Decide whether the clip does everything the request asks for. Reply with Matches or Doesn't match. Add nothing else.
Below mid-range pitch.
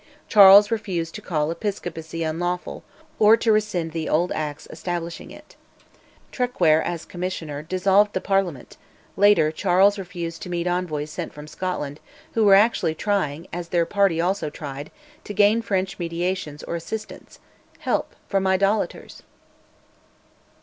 Doesn't match